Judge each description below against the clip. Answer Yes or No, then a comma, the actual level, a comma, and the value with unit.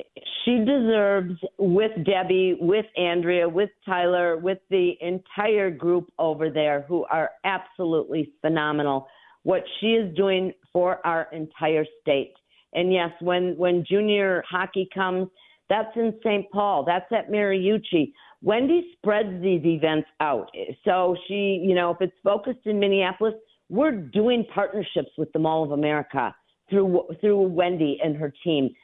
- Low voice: No, medium, 185 Hz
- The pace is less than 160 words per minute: Yes, average, 140 wpm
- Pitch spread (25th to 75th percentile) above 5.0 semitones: No, average, 3.5 semitones